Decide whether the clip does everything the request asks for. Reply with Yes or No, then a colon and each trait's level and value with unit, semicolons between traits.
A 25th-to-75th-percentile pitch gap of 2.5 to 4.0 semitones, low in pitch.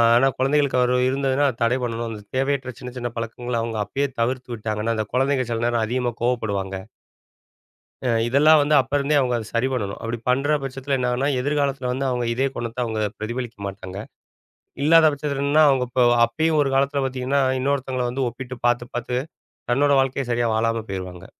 Yes: average, 2.8 semitones; low, 125 Hz